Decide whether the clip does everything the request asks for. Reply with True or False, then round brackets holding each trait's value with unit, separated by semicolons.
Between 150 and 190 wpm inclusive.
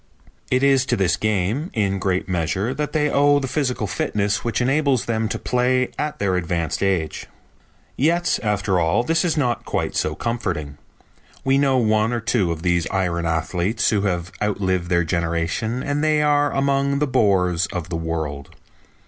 True (175 wpm)